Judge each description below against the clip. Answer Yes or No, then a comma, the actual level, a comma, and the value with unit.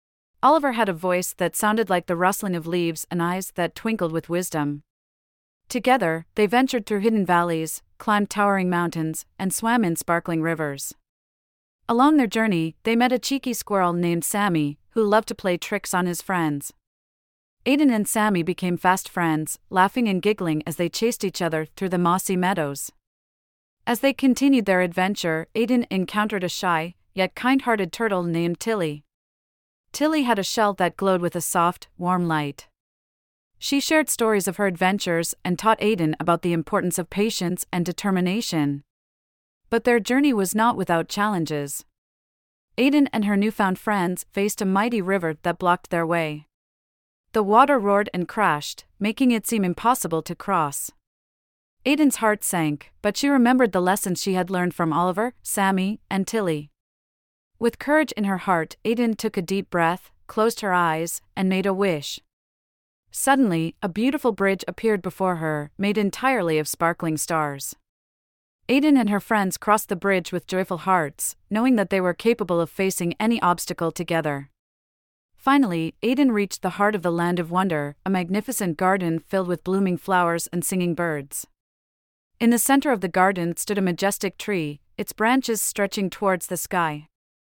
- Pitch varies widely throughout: No, average, 4.4 semitones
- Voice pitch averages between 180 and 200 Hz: Yes, medium, 185 Hz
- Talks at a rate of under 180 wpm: Yes, average, 165 wpm